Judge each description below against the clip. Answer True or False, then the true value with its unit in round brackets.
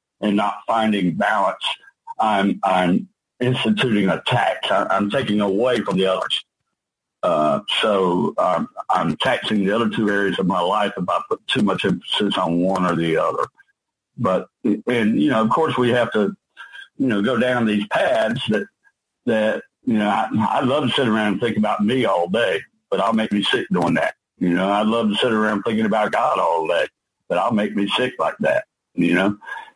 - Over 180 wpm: True (195 wpm)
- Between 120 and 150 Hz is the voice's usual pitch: False (105 Hz)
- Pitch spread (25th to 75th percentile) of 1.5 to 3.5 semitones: False (3.9 semitones)